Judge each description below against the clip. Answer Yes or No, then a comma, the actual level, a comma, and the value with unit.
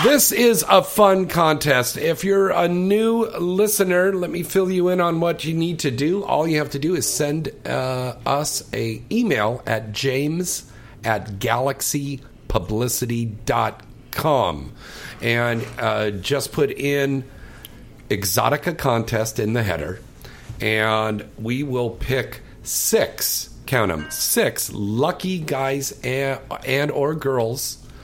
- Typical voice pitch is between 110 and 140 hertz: Yes, low, 135 Hz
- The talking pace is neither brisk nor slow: No, slow, 130 wpm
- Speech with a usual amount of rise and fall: No, wide, 6.4 semitones